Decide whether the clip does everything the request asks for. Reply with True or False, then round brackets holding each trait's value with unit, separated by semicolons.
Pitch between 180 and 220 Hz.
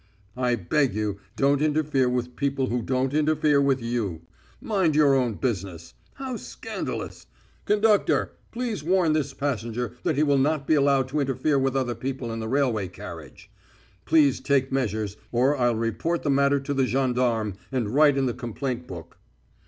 False (135 Hz)